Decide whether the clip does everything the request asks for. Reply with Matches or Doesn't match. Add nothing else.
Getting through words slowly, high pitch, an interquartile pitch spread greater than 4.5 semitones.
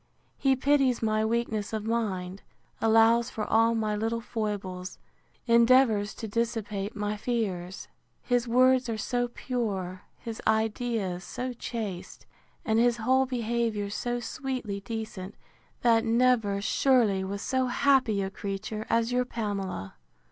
Doesn't match